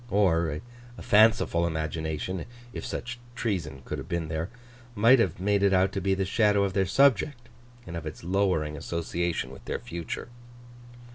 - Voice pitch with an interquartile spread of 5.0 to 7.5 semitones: Yes, average, 5.3 semitones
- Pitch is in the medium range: No, very low, 95 Hz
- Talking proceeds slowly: No, average, 155 wpm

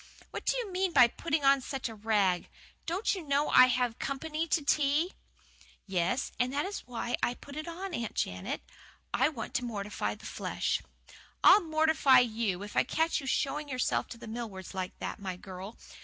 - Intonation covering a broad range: Yes, wide, 6.0 semitones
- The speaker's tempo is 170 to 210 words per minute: Yes, average, 200 wpm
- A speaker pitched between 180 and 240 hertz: No, very high, 255 Hz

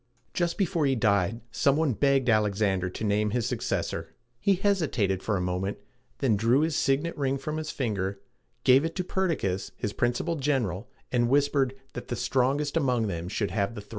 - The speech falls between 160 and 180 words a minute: No, average, 190 wpm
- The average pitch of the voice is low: Yes, low, 125 Hz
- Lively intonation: Yes, wide, 5.9 semitones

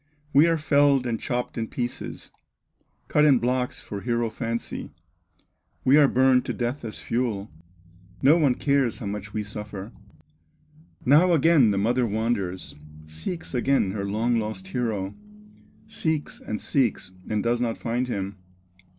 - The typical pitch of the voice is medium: No, low, 120 Hz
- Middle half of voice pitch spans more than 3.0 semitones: Yes, average, 4.3 semitones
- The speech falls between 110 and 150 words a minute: Yes, average, 145 wpm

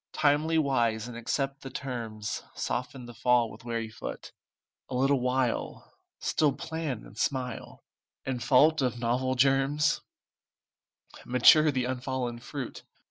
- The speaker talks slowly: Yes, slow, 125 wpm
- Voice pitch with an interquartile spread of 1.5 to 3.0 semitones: Yes, narrow, 2.6 semitones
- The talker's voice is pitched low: Yes, low, 130 Hz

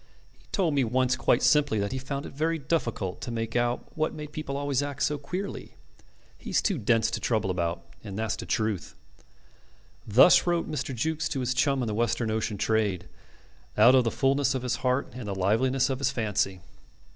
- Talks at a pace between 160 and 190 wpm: No, average, 200 wpm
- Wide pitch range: No, average, 4.4 semitones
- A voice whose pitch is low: Yes, low, 125 Hz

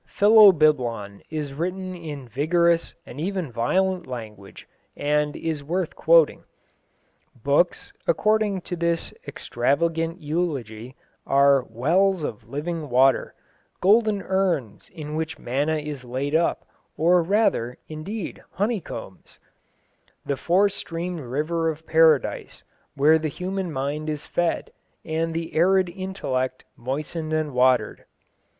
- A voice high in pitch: No, medium, 160 Hz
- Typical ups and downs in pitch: Yes, average, 4.5 semitones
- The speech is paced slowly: Yes, slow, 115 wpm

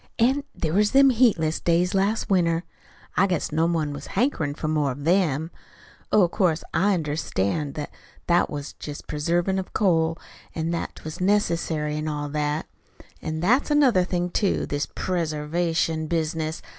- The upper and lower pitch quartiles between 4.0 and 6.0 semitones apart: No, average, 3.5 semitones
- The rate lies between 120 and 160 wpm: Yes, average, 155 wpm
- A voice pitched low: No, medium, 165 Hz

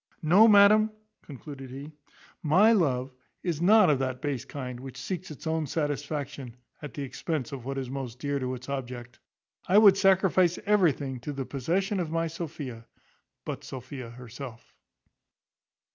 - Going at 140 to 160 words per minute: Yes, average, 155 wpm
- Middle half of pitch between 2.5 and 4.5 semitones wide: No, average, 5.1 semitones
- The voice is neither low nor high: Yes, medium, 145 Hz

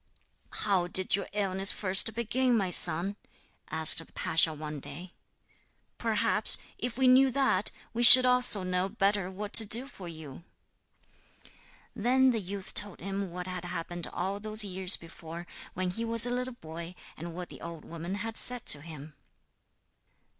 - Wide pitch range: No, average, 4.6 semitones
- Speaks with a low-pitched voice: No, high, 190 Hz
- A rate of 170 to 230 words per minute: No, average, 160 wpm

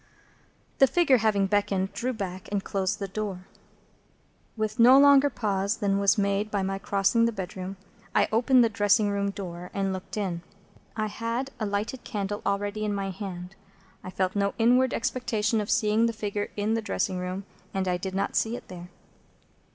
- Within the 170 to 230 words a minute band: Yes, average, 180 wpm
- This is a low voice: No, high, 205 Hz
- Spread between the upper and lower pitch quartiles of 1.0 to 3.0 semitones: Yes, narrow, 2.5 semitones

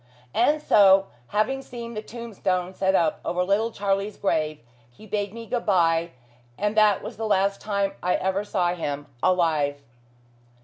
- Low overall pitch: No, high, 195 Hz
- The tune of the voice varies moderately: Yes, average, 3.2 semitones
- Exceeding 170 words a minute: No, average, 160 wpm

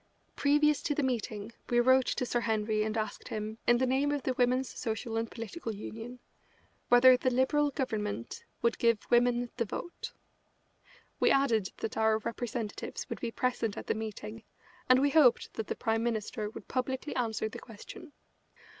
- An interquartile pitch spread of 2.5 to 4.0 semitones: Yes, average, 2.8 semitones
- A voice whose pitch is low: No, high, 240 Hz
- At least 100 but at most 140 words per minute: No, average, 170 wpm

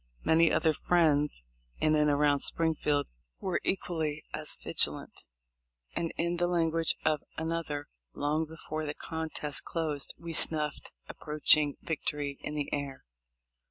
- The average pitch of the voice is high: No, medium, 155 Hz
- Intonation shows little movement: Yes, narrow, 1.9 semitones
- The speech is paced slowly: Yes, slow, 125 wpm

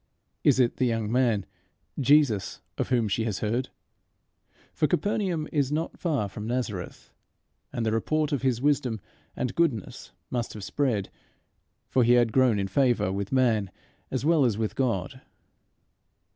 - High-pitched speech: No, low, 125 Hz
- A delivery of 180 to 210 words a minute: No, average, 155 wpm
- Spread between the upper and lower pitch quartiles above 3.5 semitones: Yes, average, 4.3 semitones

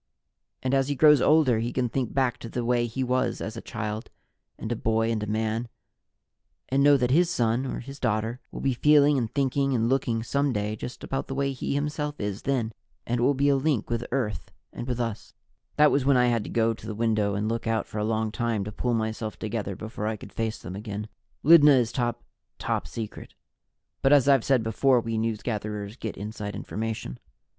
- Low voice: Yes, low, 120 Hz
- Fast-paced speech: Yes, fast, 220 wpm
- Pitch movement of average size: Yes, average, 3.5 semitones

